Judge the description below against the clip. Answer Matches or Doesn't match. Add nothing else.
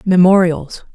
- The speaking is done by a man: Doesn't match